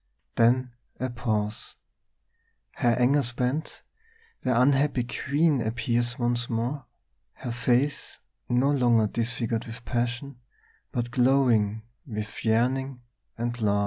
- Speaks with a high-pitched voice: No, low, 120 Hz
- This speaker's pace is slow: Yes, slow, 110 wpm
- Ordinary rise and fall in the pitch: No, narrow, 2.0 semitones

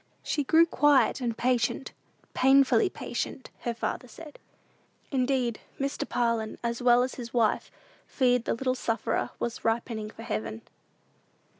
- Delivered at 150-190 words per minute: No, slow, 135 wpm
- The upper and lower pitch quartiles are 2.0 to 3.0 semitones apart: Yes, narrow, 2.5 semitones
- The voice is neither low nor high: No, high, 245 Hz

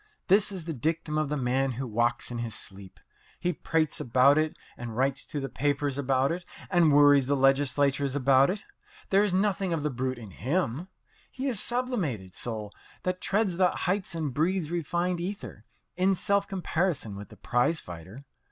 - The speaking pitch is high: No, medium, 145 Hz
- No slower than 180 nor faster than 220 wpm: Yes, average, 185 wpm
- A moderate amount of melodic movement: No, wide, 5.8 semitones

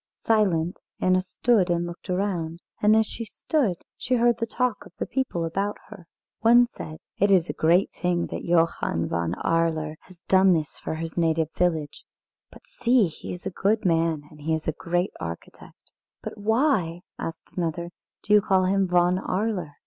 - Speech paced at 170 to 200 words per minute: Yes, average, 180 wpm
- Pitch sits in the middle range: Yes, medium, 180 Hz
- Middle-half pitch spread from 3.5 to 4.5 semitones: Yes, average, 4.0 semitones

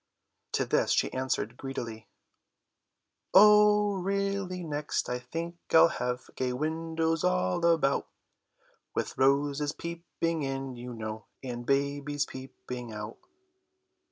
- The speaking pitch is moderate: Yes, medium, 145 Hz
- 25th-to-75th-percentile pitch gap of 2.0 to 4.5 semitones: No, average, 5.1 semitones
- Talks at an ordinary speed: No, slow, 110 wpm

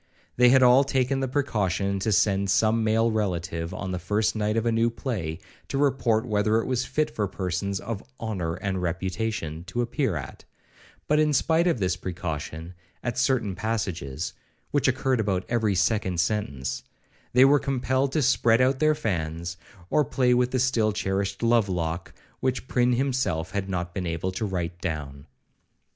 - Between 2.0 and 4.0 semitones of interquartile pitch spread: No, wide, 5.5 semitones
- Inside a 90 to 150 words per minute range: No, average, 175 wpm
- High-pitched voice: No, low, 110 Hz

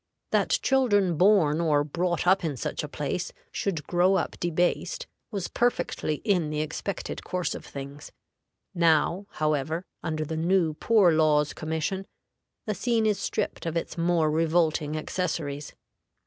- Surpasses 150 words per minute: No, average, 145 wpm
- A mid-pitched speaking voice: Yes, medium, 170 Hz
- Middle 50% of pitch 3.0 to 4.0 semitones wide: Yes, average, 3.5 semitones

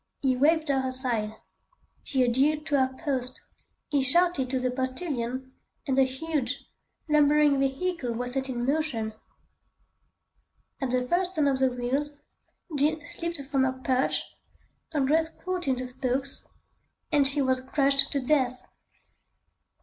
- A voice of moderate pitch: No, very high, 270 Hz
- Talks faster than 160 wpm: No, average, 140 wpm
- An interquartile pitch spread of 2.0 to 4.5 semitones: Yes, narrow, 2.6 semitones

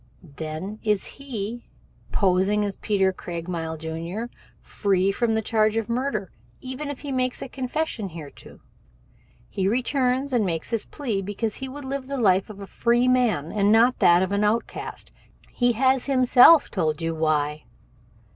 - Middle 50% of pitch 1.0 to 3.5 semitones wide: No, wide, 5.5 semitones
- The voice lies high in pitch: Yes, high, 215 Hz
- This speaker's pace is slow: No, average, 155 wpm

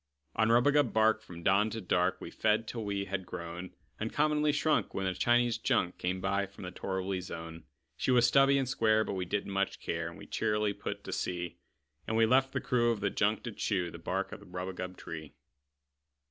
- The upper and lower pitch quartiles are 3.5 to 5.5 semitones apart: Yes, average, 3.9 semitones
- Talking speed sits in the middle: No, fast, 215 wpm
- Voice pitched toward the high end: No, low, 100 Hz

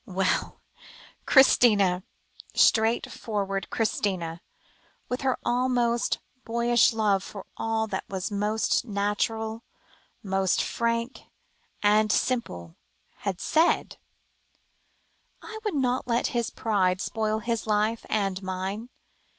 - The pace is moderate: No, slow, 100 wpm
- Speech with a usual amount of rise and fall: Yes, average, 3.1 semitones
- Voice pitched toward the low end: No, high, 220 Hz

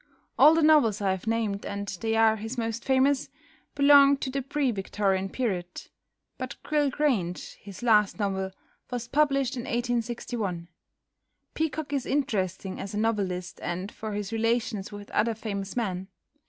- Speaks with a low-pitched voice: No, high, 225 Hz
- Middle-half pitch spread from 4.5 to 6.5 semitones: Yes, average, 4.9 semitones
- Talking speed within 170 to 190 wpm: No, average, 155 wpm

